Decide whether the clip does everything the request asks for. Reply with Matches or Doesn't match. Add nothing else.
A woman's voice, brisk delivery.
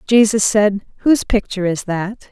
Doesn't match